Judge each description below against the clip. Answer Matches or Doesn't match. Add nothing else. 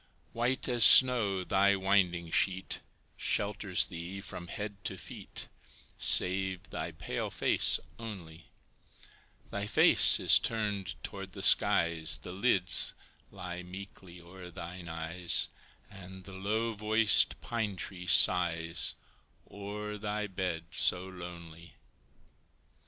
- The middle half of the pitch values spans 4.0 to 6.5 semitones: Doesn't match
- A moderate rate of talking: Doesn't match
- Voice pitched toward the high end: Doesn't match